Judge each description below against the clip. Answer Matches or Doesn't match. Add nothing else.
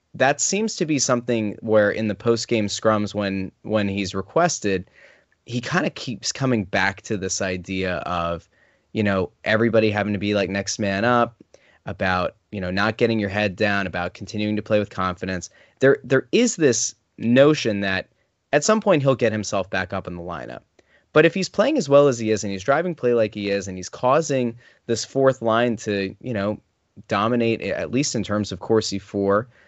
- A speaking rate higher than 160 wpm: Matches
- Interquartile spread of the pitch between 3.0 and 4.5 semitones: Matches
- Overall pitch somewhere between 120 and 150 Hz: Doesn't match